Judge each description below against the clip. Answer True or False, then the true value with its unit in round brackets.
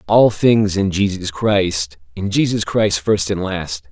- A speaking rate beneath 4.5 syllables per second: True (3.7 syllables/s)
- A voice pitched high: False (95 Hz)